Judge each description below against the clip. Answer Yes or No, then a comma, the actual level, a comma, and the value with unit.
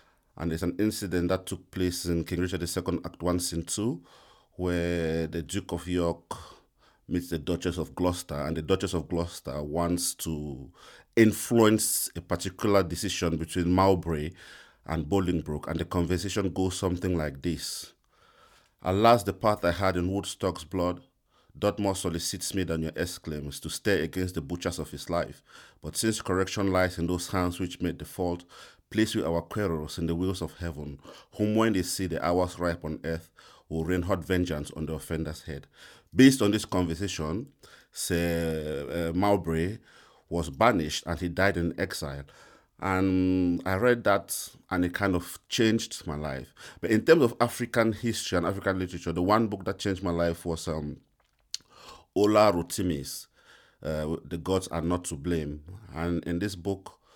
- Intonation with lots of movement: No, narrow, 2.6 semitones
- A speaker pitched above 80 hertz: Yes, very low, 90 Hz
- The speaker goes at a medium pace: Yes, average, 170 wpm